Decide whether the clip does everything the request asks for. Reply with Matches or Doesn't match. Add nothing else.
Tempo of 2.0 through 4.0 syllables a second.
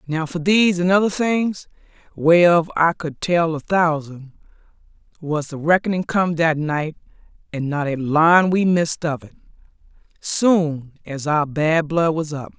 Matches